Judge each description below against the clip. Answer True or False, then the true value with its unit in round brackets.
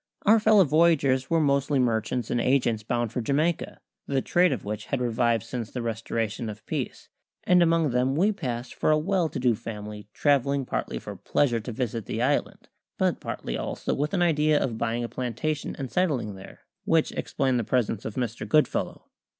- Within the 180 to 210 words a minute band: True (190 wpm)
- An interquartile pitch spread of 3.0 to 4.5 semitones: False (4.9 semitones)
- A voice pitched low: True (130 Hz)